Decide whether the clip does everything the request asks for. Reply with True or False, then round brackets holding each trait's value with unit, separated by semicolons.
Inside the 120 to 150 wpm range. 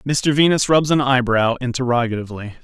True (135 wpm)